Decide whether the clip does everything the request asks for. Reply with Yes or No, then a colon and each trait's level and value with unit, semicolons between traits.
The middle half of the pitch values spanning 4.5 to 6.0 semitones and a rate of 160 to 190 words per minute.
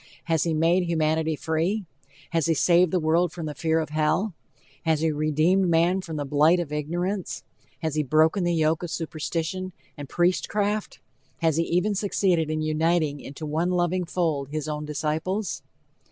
No: narrow, 2.4 semitones; average, 175 wpm